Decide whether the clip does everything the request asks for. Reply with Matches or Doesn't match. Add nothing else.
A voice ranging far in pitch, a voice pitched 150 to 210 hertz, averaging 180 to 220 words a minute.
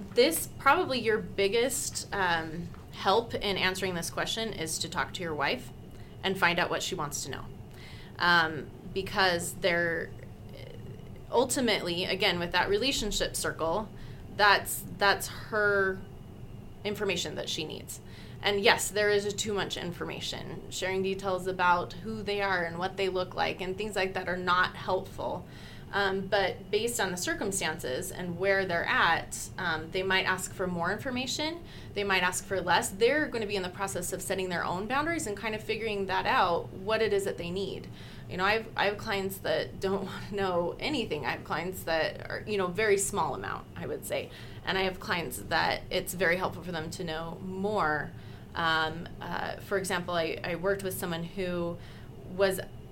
Doesn't match